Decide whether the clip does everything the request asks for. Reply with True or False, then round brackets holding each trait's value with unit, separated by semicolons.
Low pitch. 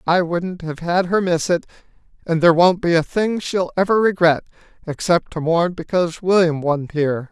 False (170 Hz)